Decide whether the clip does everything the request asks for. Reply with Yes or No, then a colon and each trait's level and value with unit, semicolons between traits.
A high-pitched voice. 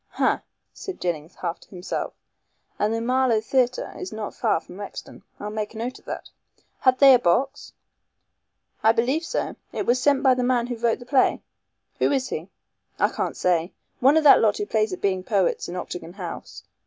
Yes: high, 225 Hz